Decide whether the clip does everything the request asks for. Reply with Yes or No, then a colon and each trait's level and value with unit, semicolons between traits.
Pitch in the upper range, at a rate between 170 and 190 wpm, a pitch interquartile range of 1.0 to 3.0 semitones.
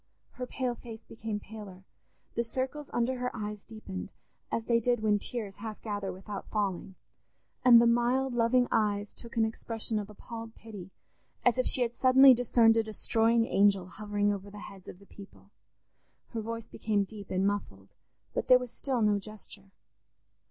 Yes: high, 220 Hz; average, 175 wpm; average, 2.7 semitones